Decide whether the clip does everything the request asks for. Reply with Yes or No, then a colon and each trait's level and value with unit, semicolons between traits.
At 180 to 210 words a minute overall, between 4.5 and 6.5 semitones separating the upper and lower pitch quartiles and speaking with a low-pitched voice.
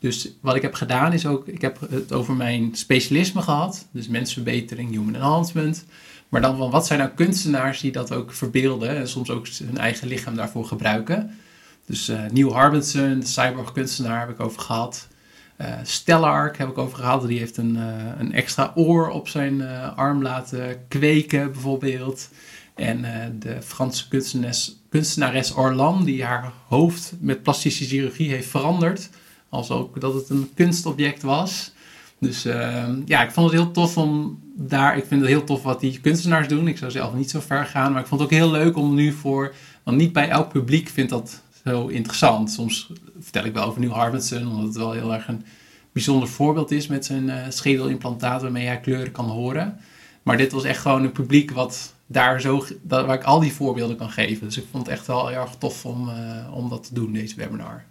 No: fast, 200 wpm; average, 3.3 semitones; low, 130 Hz